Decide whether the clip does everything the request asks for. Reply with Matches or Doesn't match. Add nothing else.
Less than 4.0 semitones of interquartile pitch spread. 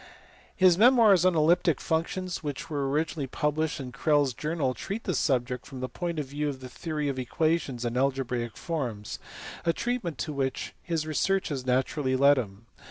Doesn't match